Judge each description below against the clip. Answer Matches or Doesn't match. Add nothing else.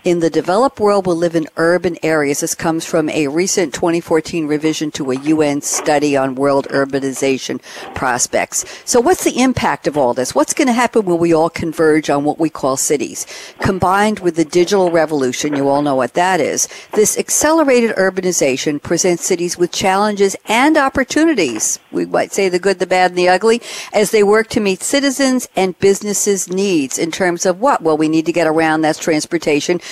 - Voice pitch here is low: Doesn't match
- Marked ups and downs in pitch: Doesn't match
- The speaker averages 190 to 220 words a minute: Matches